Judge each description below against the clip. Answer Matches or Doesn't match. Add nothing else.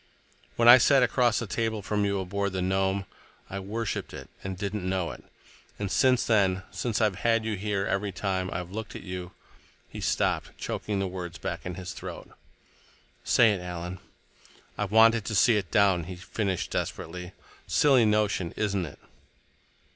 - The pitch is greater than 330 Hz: Doesn't match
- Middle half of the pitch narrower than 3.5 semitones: Matches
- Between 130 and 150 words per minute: Doesn't match